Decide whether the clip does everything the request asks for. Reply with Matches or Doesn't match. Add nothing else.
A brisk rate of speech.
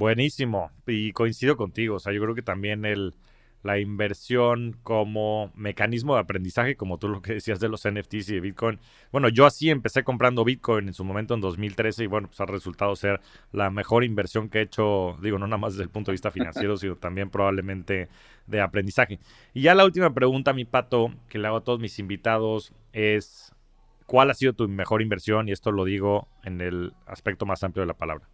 Matches